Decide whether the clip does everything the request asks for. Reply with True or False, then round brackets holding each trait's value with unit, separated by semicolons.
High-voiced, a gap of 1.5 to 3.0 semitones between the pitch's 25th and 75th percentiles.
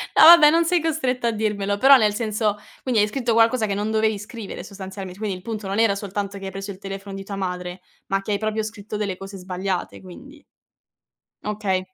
True (205 Hz; 2.5 semitones)